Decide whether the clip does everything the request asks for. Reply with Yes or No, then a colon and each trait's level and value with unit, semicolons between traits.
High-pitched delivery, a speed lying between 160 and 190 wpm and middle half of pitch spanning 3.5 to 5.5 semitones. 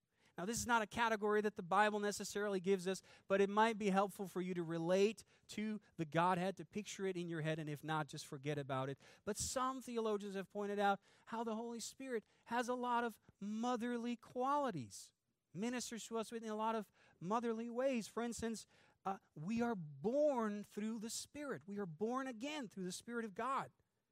No: high, 210 Hz; average, 200 wpm; average, 3.8 semitones